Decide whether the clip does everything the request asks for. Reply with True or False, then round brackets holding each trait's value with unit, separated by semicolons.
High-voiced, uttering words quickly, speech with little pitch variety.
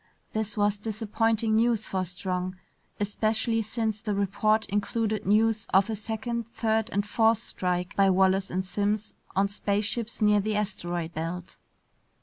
False (210 Hz; 140 wpm; 2.3 semitones)